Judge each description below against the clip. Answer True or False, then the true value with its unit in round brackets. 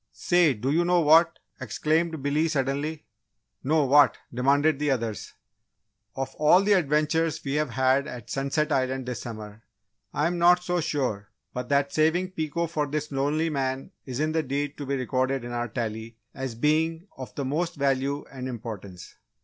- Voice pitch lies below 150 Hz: True (140 Hz)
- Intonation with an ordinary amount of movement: True (3.4 semitones)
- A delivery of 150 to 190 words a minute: True (165 wpm)